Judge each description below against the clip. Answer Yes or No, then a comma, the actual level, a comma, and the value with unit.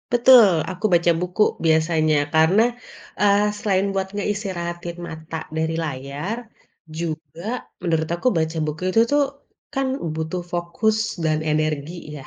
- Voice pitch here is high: No, medium, 170 Hz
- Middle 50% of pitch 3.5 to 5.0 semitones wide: Yes, average, 3.9 semitones